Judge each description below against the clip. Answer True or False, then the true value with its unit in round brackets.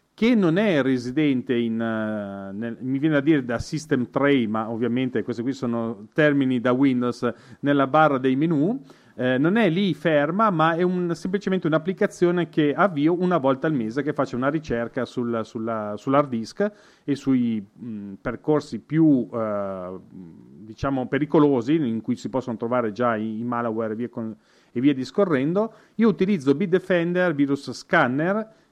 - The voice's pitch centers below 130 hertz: False (135 Hz)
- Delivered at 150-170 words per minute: True (160 wpm)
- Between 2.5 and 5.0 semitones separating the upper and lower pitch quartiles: False (5.5 semitones)